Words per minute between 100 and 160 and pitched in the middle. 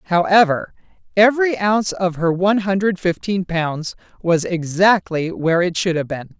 Yes: average, 150 wpm; medium, 180 Hz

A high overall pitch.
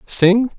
Yes: high, 215 Hz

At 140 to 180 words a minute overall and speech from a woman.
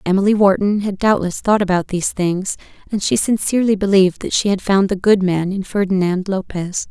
No: average, 190 wpm; female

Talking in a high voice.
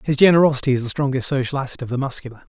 No: low, 135 Hz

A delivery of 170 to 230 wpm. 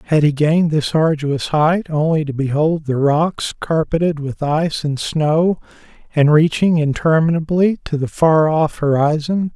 No: average, 150 wpm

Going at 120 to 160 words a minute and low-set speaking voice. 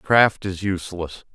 Yes: slow, 135 wpm; very low, 95 Hz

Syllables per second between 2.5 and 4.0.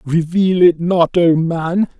Yes: 3.5 syllables/s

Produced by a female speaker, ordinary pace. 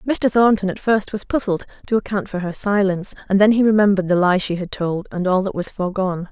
No: female; fast, 235 wpm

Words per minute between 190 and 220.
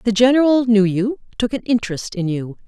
Yes: average, 200 wpm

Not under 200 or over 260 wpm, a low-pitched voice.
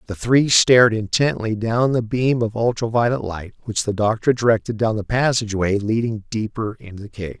No: average, 185 wpm; low, 110 Hz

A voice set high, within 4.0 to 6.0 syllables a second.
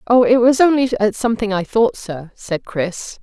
Yes: high, 220 Hz; 4.8 syllables/s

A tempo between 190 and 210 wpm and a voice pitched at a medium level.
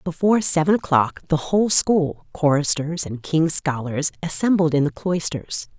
No: average, 145 wpm; medium, 160 Hz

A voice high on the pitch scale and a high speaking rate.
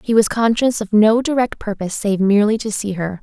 Yes: high, 215 Hz; fast, 225 wpm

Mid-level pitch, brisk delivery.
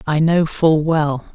No: medium, 155 Hz; average, 180 wpm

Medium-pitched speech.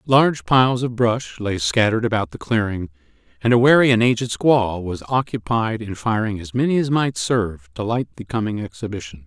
No: low, 110 Hz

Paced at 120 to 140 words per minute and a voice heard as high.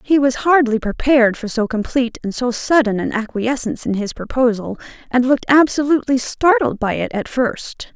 No: average, 175 wpm; very high, 250 Hz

